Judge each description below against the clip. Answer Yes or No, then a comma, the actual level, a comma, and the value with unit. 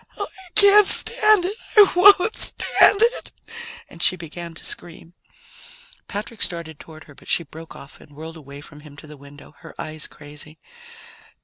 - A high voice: No, medium, 165 Hz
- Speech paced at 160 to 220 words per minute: Yes, average, 175 wpm